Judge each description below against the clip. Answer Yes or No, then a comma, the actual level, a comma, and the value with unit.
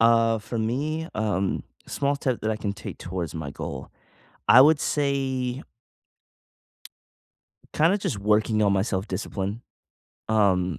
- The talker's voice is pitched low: Yes, low, 110 Hz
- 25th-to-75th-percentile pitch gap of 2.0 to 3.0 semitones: No, average, 4.9 semitones